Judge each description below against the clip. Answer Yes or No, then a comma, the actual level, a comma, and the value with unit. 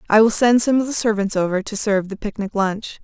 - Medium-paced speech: No, fast, 255 wpm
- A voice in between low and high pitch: No, high, 210 Hz